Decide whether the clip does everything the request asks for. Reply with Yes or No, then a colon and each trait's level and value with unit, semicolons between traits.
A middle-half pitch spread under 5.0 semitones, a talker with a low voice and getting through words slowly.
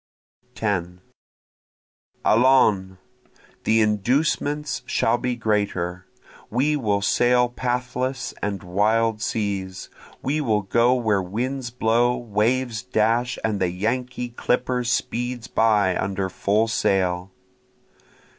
Yes: average, 3.7 semitones; low, 115 Hz; slow, 100 wpm